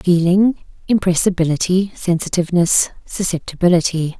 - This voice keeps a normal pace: No, slow, 55 wpm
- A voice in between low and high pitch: Yes, medium, 175 Hz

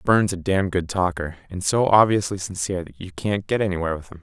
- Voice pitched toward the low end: Yes, very low, 95 Hz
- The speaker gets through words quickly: Yes, fast, 225 wpm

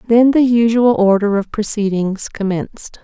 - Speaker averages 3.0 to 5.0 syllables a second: Yes, 4.7 syllables/s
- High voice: Yes, high, 215 Hz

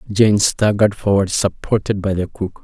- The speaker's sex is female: No, male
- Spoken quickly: No, average, 160 wpm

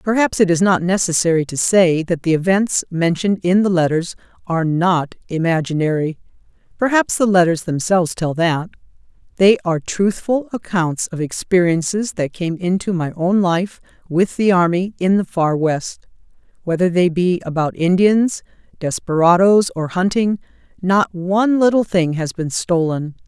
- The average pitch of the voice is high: No, medium, 180 Hz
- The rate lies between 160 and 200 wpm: No, average, 140 wpm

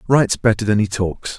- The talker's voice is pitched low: Yes, low, 110 Hz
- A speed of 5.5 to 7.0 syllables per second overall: Yes, 5.7 syllables/s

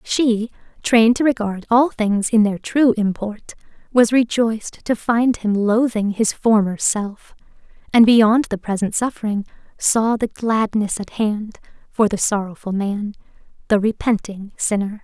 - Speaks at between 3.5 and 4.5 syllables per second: Yes, 4.2 syllables/s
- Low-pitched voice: No, high, 220 Hz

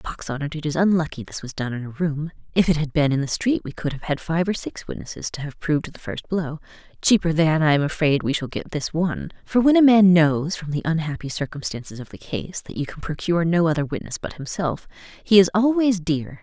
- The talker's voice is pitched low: No, medium, 160 Hz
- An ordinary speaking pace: No, fast, 245 wpm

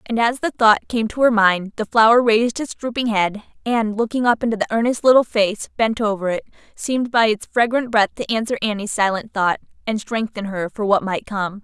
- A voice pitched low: No, high, 220 Hz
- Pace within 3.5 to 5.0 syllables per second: No, 5.4 syllables/s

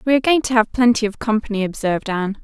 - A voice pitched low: No, high, 225 Hz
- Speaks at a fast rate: Yes, fast, 245 wpm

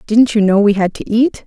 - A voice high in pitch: Yes, high, 215 Hz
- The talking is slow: No, fast, 285 wpm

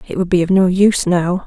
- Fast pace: Yes, fast, 285 wpm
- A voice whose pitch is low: No, medium, 180 Hz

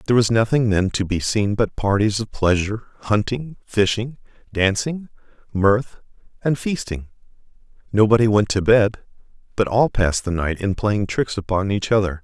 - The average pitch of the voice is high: No, low, 105 Hz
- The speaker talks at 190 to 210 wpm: No, average, 155 wpm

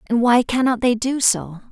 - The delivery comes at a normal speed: No, fast, 210 wpm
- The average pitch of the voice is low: No, high, 235 Hz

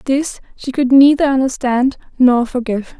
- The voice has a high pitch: Yes, very high, 260 Hz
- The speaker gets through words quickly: No, average, 140 wpm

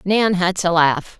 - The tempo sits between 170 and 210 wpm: Yes, average, 200 wpm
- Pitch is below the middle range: No, medium, 180 Hz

